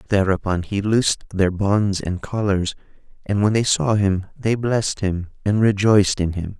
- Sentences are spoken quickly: No, average, 175 wpm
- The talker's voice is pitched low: Yes, low, 100 Hz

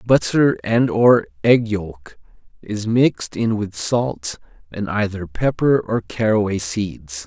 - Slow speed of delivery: Yes, slow, 130 wpm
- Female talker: No, male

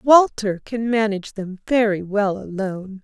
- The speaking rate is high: No, average, 140 wpm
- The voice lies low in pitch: No, high, 210 Hz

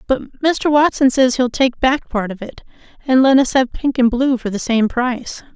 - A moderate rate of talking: No, fast, 225 wpm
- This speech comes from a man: No, female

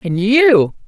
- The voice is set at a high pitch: Yes, high, 200 Hz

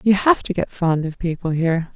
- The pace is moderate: No, fast, 245 wpm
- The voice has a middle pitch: Yes, medium, 175 Hz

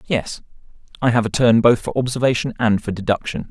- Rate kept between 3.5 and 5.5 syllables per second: No, 5.8 syllables/s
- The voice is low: Yes, low, 115 Hz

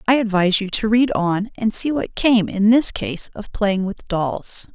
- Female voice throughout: Yes, female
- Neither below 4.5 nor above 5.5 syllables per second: No, 4.3 syllables/s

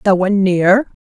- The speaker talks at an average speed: Yes, average, 175 wpm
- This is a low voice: No, high, 195 Hz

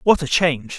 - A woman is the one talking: No, male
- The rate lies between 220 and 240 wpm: Yes, fast, 230 wpm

